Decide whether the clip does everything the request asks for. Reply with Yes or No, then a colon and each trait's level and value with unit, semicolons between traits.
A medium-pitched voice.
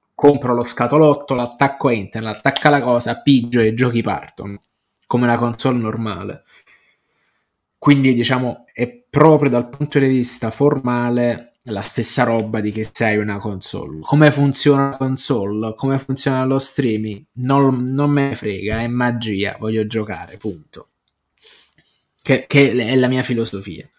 No: low, 120 Hz